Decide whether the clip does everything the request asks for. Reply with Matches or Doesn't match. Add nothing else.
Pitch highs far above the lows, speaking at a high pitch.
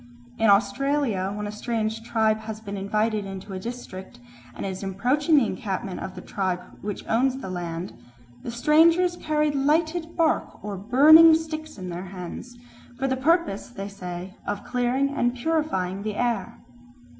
Matches